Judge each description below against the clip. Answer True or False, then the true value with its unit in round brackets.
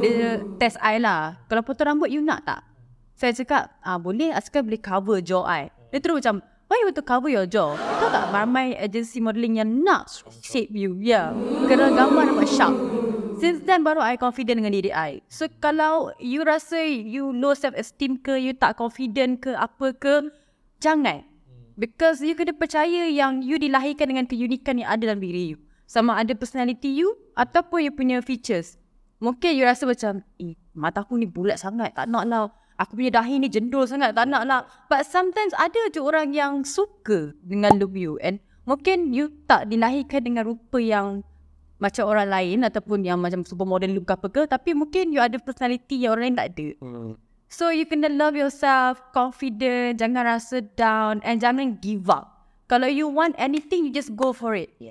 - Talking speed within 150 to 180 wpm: False (190 wpm)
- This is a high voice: True (245 Hz)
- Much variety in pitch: False (5.0 semitones)